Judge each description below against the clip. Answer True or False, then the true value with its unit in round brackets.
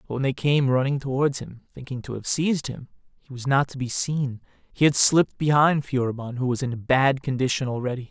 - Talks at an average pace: False (220 wpm)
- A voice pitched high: False (135 Hz)